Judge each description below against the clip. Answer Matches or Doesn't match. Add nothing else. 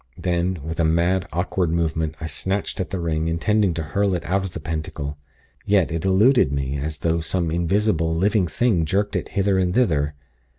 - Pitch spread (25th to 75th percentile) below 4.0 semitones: Matches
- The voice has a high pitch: Doesn't match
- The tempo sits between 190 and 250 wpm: Matches